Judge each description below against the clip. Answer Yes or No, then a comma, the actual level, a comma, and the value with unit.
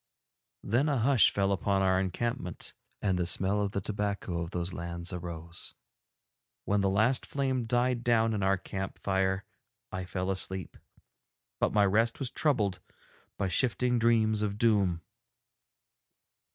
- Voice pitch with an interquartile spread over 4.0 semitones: No, average, 3.7 semitones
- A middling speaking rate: Yes, average, 145 wpm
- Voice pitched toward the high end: No, low, 100 Hz